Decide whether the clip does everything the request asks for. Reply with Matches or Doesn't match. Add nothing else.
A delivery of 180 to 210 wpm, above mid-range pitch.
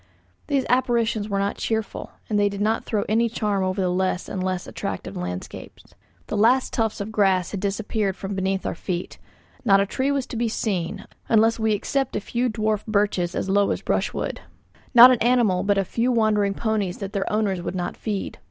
Matches